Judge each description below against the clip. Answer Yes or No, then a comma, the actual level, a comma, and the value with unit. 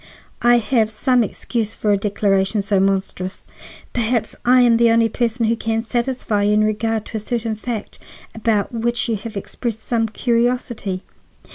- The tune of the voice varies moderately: No, narrow, 2.2 semitones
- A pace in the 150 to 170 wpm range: Yes, average, 165 wpm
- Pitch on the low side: No, high, 225 Hz